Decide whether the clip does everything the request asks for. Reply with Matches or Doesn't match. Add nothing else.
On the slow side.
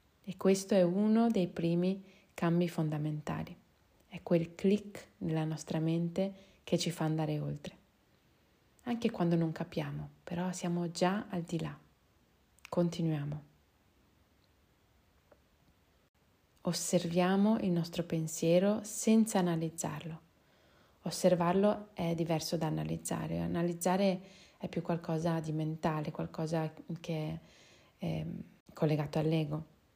Matches